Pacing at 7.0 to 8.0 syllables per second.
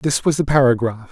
No: 5.6 syllables/s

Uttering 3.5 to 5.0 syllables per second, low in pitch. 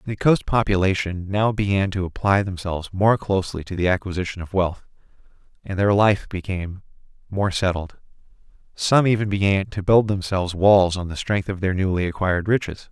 No: 5.5 syllables/s; very low, 95 Hz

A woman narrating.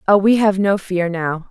Yes: female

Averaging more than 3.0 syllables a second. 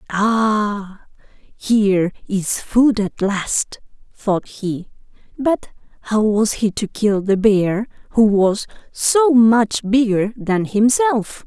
No: 2.9 syllables/s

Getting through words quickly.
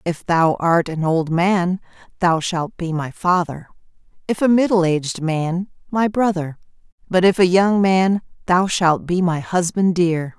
No: average, 170 wpm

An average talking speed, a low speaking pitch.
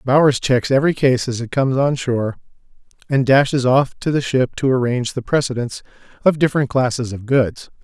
Yes: average, 185 wpm; low, 130 Hz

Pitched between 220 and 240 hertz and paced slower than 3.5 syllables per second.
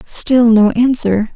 Yes: high, 230 Hz; 3.2 syllables/s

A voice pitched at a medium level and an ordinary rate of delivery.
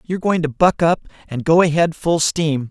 No: medium, 160 Hz; fast, 220 wpm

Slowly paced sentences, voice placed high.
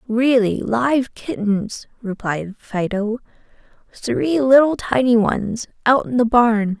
Yes: slow, 115 wpm; high, 230 Hz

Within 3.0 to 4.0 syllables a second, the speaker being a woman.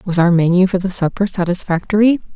No: 6.2 syllables/s; female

